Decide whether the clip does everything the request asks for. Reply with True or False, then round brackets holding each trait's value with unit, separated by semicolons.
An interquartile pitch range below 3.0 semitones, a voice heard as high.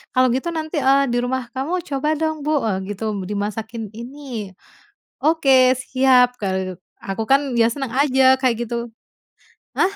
False (3.6 semitones; 255 Hz)